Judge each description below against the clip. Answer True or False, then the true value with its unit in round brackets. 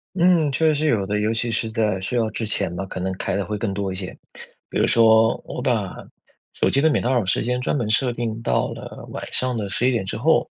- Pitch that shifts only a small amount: False (3.8 semitones)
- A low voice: True (115 Hz)